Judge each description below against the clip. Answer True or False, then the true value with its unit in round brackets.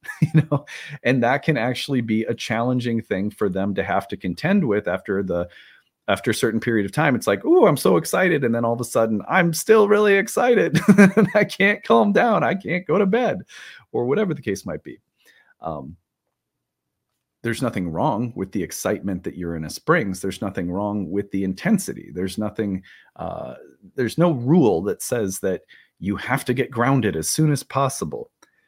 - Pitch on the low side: True (120 Hz)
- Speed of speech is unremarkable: True (195 wpm)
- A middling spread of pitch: False (8.3 semitones)